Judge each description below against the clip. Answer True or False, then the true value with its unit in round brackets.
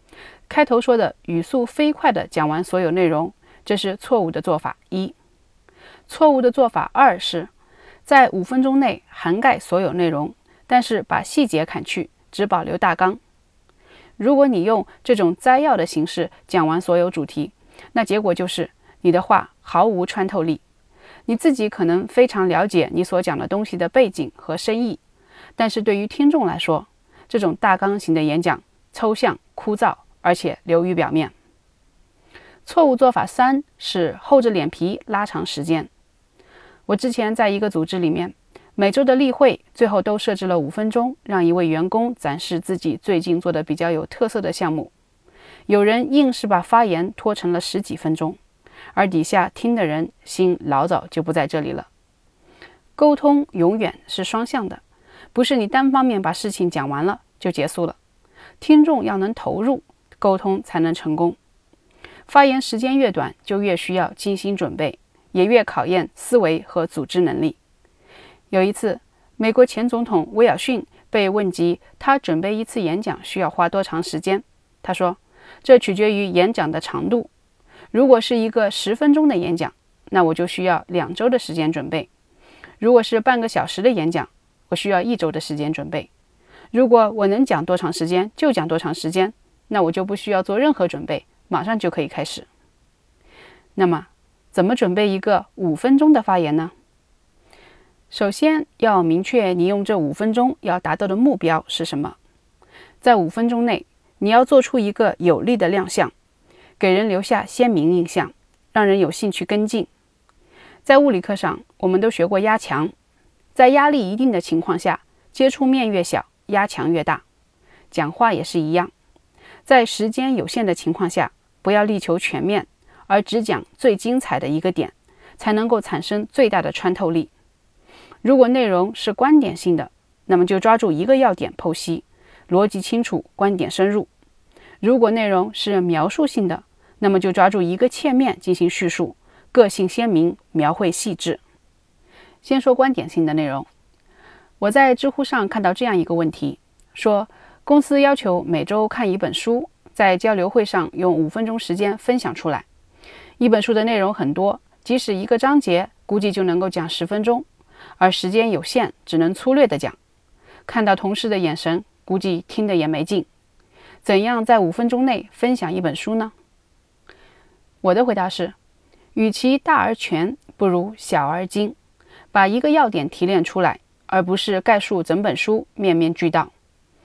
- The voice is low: False (195 Hz)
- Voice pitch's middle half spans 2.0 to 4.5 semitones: False (5.3 semitones)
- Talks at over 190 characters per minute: True (250 characters per minute)